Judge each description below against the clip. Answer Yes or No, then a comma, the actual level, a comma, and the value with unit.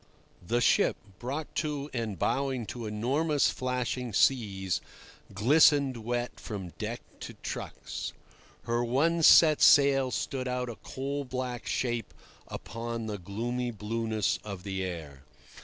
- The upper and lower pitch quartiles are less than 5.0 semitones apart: Yes, average, 4.0 semitones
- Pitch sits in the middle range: No, low, 120 Hz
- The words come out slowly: Yes, slow, 125 wpm